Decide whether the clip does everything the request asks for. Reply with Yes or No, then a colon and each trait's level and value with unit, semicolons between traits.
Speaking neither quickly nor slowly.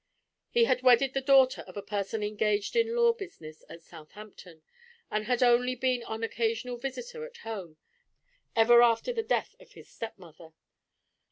Yes: average, 160 wpm